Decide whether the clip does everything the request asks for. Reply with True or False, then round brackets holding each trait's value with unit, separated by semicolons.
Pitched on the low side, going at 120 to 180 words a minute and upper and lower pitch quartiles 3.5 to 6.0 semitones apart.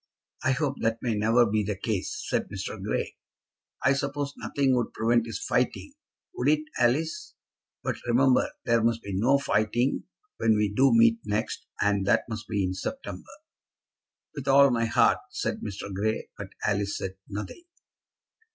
True (115 Hz; 160 wpm; 4.1 semitones)